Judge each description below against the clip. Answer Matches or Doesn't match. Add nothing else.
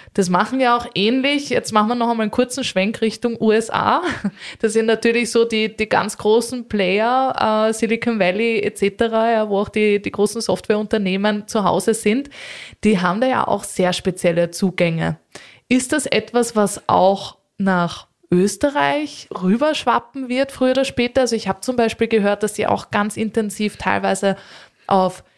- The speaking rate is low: Doesn't match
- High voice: Matches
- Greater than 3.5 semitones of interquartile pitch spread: Doesn't match